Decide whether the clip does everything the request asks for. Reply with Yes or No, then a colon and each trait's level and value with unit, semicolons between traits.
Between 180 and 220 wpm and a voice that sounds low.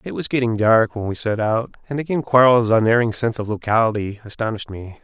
Yes: fast, 205 wpm; low, 115 Hz